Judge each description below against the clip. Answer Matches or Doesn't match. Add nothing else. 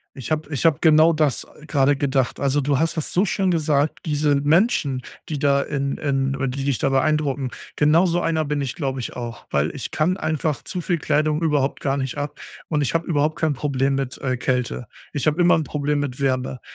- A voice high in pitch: Doesn't match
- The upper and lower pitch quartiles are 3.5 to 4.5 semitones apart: Doesn't match